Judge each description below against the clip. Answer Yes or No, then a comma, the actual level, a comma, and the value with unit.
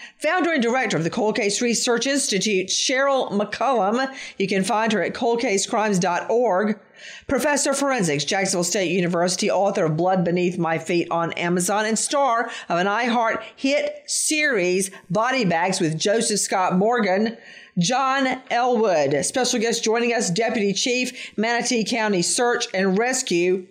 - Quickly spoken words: No, average, 145 wpm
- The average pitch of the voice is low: No, high, 215 Hz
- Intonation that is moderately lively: Yes, average, 4.8 semitones